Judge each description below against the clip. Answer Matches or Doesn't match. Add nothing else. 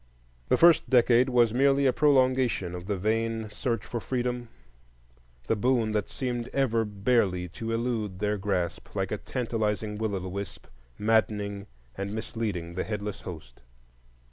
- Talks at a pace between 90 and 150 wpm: Matches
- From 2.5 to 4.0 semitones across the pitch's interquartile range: Matches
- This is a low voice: Matches